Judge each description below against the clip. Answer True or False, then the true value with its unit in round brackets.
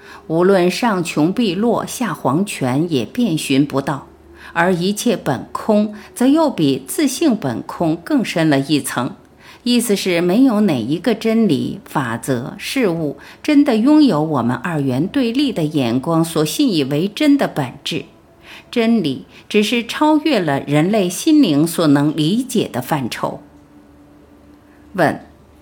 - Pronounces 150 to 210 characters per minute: True (200 characters per minute)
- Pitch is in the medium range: True (180 Hz)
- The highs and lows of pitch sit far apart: True (8.4 semitones)